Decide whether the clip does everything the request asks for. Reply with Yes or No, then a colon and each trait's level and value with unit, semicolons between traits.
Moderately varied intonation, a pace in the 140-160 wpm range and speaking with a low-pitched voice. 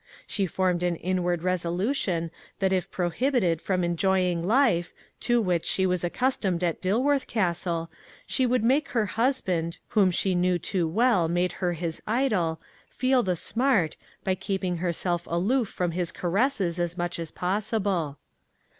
No: average, 3.9 semitones; average, 150 wpm; medium, 185 Hz